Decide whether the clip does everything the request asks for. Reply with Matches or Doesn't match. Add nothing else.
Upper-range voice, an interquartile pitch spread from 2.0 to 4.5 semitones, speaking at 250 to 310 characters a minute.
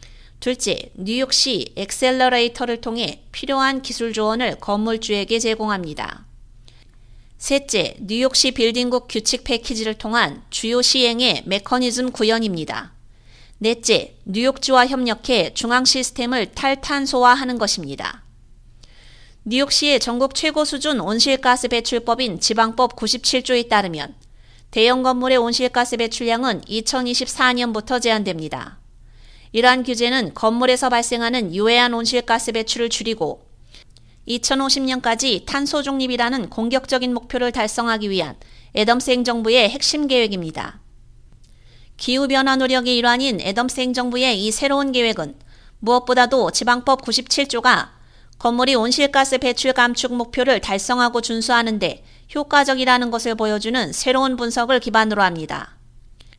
Matches